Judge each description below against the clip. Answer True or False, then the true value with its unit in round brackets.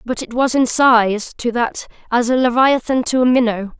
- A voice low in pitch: False (245 Hz)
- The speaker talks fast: False (190 wpm)